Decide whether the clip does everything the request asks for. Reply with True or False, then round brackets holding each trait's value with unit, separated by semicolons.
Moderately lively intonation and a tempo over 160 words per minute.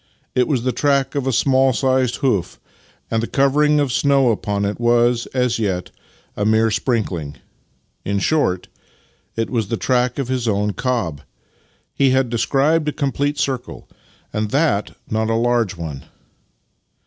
False (3.9 semitones; 155 wpm)